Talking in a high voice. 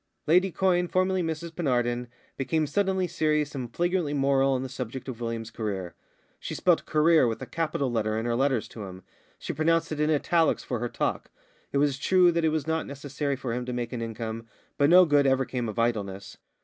No: medium, 140 Hz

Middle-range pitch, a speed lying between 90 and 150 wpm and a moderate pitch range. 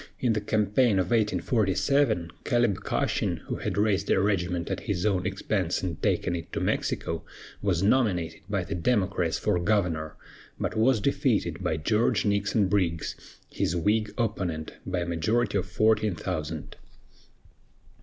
No: very low, 95 Hz; average, 145 wpm; average, 3.7 semitones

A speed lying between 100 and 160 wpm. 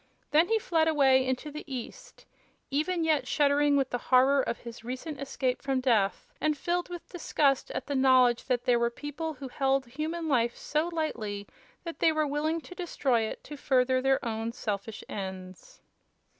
No: average, 180 wpm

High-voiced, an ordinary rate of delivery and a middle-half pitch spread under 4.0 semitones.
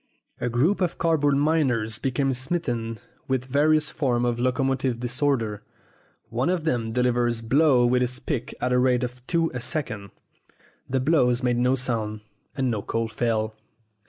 No: low, 125 Hz; average, 160 wpm; average, 2.7 semitones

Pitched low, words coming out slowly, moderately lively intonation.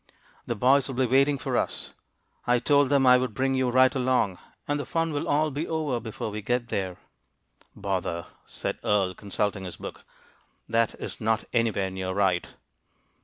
No: low, 120 Hz; average, 175 wpm; average, 4.9 semitones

